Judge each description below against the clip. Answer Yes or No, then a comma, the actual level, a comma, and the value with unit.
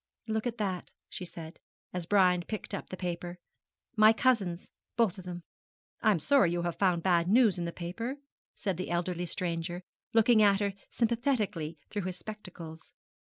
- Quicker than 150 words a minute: Yes, average, 170 wpm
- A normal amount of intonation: Yes, average, 3.8 semitones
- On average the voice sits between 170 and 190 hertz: Yes, medium, 185 Hz